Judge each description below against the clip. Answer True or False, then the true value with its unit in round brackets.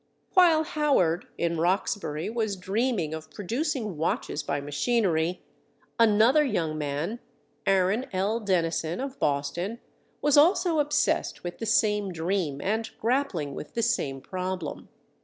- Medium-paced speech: False (120 wpm)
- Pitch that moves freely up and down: True (6.4 semitones)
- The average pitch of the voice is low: False (195 Hz)